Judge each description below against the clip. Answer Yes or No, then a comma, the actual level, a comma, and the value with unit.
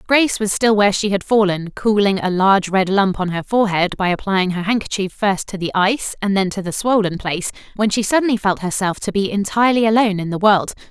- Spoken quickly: Yes, fast, 225 wpm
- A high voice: Yes, high, 200 Hz